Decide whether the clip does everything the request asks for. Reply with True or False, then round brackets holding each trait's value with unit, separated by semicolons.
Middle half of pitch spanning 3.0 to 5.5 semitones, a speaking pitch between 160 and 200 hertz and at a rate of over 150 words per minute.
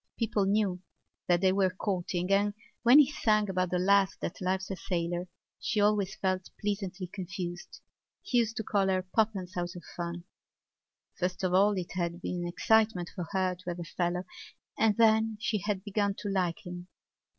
False (2.5 semitones; 190 Hz; 185 wpm)